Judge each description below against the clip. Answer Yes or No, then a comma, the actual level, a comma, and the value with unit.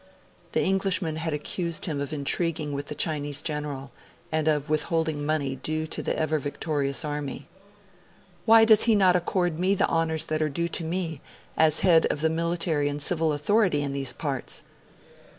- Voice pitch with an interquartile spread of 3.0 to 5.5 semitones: No, narrow, 2.5 semitones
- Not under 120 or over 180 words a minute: Yes, average, 175 wpm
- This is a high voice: No, medium, 155 Hz